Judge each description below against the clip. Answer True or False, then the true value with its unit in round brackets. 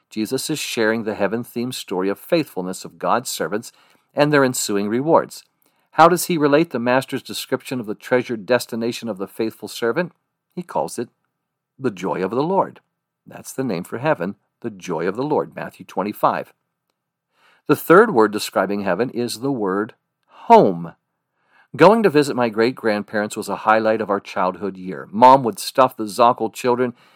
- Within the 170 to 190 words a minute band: True (175 wpm)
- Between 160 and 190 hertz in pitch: False (115 Hz)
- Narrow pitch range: False (3.7 semitones)